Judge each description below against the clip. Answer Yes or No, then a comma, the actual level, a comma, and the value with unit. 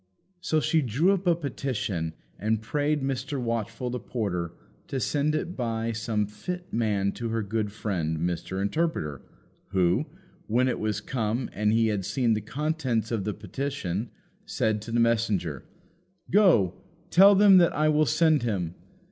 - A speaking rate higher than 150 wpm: Yes, average, 160 wpm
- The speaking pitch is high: No, low, 115 Hz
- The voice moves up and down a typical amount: No, wide, 5.8 semitones